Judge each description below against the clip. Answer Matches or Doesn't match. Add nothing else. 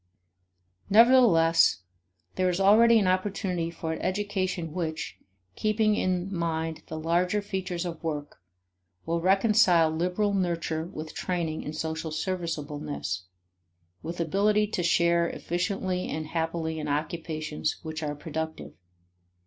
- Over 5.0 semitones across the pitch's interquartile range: Doesn't match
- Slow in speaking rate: Matches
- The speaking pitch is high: Doesn't match